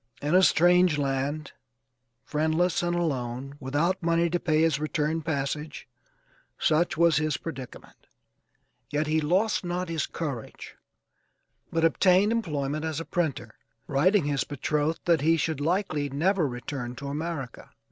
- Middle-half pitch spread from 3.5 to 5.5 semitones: No, average, 3.0 semitones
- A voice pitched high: No, medium, 155 Hz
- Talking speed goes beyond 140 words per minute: No, slow, 135 wpm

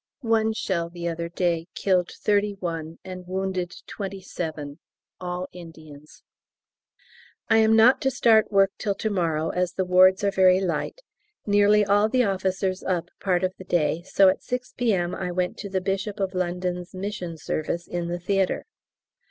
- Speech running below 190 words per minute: Yes, average, 170 wpm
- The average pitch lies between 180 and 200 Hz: Yes, medium, 185 Hz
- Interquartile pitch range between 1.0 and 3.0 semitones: Yes, narrow, 2.5 semitones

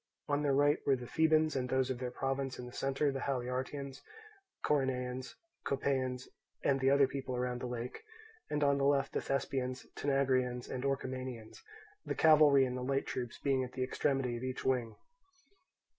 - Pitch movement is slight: Yes, narrow, 1.6 semitones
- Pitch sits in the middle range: No, low, 130 Hz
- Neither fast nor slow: Yes, average, 175 wpm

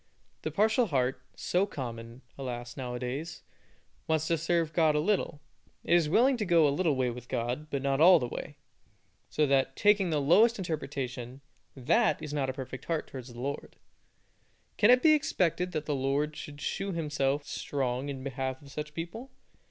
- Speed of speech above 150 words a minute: Yes, average, 185 wpm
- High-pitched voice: No, medium, 145 Hz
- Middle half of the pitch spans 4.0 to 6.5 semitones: Yes, average, 4.5 semitones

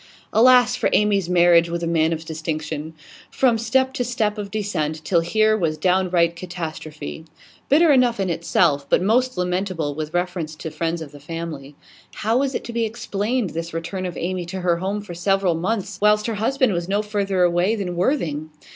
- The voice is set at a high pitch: No, medium, 180 Hz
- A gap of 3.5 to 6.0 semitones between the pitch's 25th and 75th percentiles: Yes, average, 4.3 semitones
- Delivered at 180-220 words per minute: Yes, average, 190 wpm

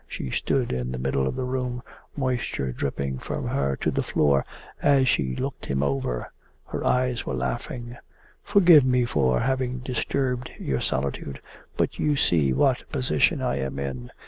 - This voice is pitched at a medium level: No, very low, 70 Hz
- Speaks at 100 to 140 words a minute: No, average, 170 wpm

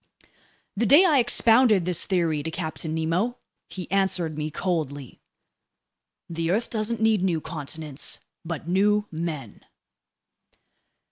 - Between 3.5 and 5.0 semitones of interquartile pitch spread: Yes, average, 4.7 semitones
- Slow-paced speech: Yes, slow, 120 wpm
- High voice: No, medium, 175 Hz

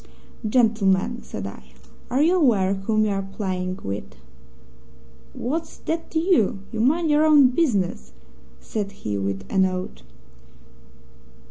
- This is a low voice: No, high, 210 Hz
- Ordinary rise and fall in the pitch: No, wide, 6.7 semitones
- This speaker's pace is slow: Yes, slow, 130 wpm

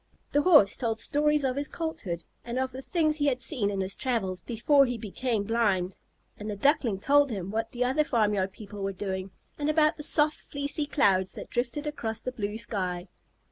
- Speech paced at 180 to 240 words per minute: Yes, average, 200 wpm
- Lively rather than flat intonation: Yes, wide, 6.2 semitones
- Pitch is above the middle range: Yes, high, 235 Hz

